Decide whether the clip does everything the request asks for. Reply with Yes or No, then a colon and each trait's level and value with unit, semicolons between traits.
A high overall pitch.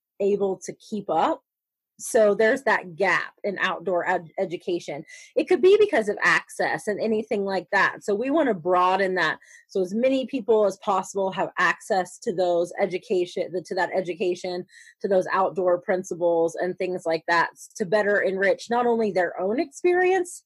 Yes: high, 195 Hz